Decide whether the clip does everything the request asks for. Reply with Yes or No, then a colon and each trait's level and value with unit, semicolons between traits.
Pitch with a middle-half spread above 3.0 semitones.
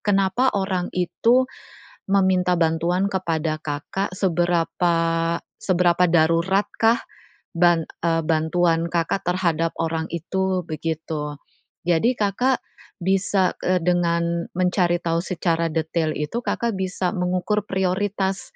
No: narrow, 2.5 semitones